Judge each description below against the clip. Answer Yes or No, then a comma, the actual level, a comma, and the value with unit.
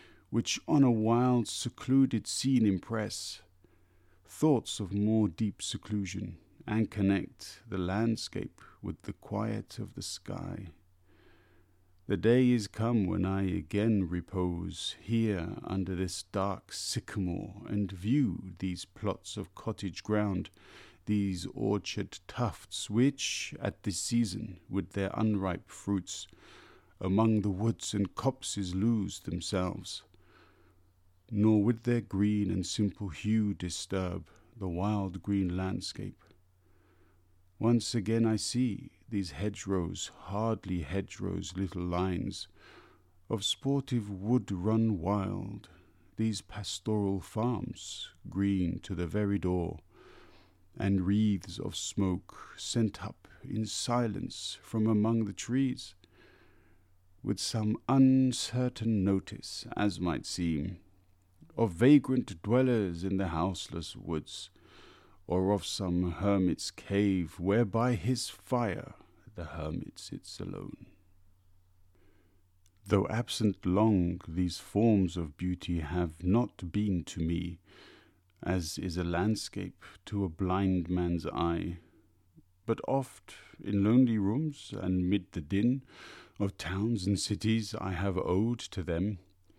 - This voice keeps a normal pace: No, slow, 115 wpm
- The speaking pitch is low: Yes, low, 100 Hz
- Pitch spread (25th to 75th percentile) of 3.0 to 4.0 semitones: Yes, average, 3.3 semitones